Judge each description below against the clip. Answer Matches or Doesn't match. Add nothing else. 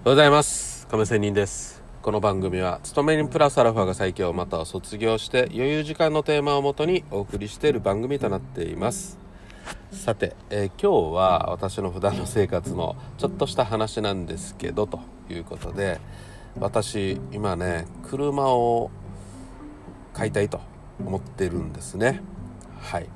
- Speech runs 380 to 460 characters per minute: Doesn't match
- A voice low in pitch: Matches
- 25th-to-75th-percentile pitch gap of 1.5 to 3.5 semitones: Doesn't match